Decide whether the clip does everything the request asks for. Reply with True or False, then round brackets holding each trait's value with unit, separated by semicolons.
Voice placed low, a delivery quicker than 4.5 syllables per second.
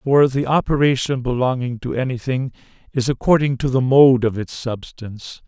True (130 Hz; 5.1 syllables/s)